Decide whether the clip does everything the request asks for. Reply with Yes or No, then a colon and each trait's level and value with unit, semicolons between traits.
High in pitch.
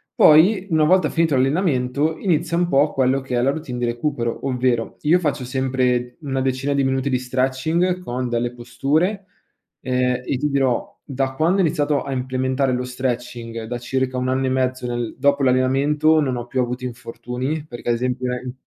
No: low, 130 Hz